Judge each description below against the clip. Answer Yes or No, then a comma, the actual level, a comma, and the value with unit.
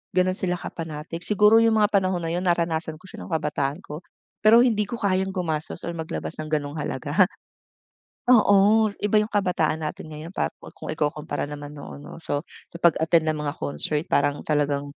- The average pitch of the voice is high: No, medium, 165 Hz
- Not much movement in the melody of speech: No, average, 4.3 semitones